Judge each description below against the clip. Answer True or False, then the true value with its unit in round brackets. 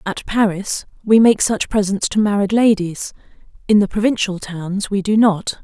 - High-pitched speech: True (200 Hz)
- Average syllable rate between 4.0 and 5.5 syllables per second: True (4.6 syllables/s)